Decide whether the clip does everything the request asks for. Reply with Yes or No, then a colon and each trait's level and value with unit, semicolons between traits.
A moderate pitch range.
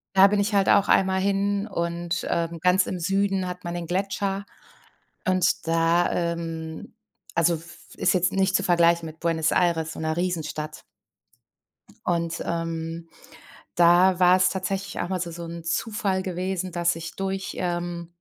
No: narrow, 2.2 semitones